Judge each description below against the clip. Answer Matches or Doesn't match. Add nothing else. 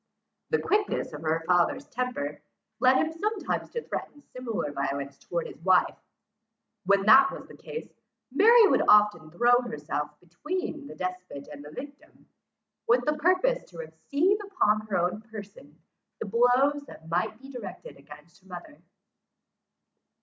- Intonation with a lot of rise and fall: Matches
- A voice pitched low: Doesn't match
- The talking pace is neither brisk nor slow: Matches